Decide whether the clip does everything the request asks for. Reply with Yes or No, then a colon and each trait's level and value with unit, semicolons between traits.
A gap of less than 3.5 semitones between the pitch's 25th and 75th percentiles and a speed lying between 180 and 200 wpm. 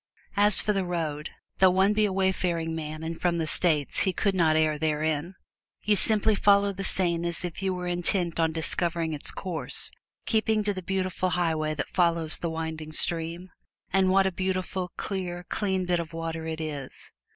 Yes: average, 2.8 semitones; average, 185 wpm